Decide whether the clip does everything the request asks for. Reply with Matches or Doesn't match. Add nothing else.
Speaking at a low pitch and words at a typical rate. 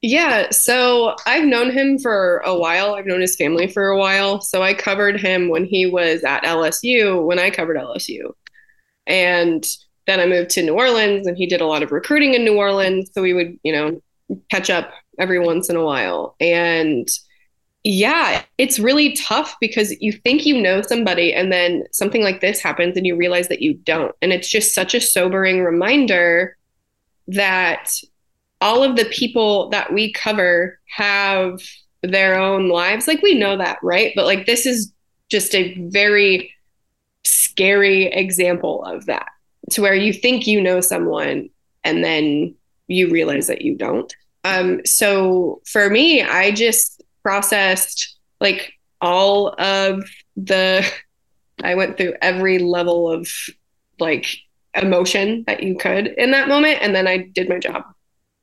Doesn't match